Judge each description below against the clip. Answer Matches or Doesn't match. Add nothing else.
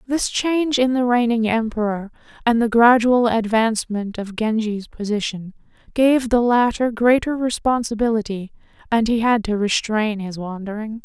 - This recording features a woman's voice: Matches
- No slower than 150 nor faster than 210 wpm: Doesn't match